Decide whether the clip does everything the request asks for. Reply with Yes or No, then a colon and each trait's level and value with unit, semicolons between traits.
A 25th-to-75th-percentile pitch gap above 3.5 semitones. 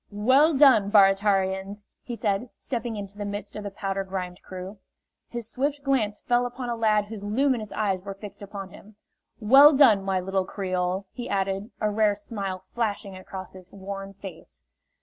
No: average, 2.9 semitones